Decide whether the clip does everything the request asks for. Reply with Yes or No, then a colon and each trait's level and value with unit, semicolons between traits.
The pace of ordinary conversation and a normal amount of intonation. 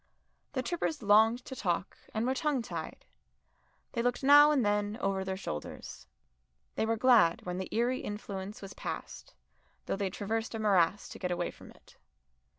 Yes: average, 170 wpm; average, 4.2 semitones